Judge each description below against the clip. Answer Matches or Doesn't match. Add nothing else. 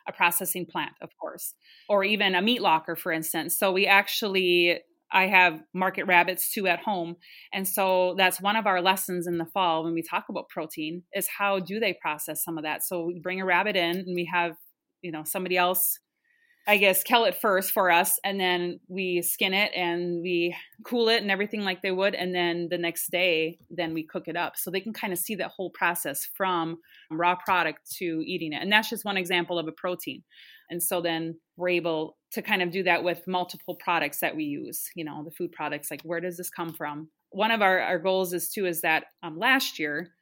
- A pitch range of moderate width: Doesn't match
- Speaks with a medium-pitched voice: Matches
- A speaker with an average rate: Doesn't match